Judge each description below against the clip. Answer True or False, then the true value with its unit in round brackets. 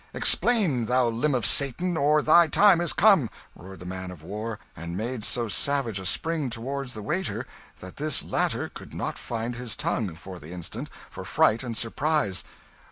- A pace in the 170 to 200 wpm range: True (180 wpm)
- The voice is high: False (120 Hz)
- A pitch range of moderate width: False (7.1 semitones)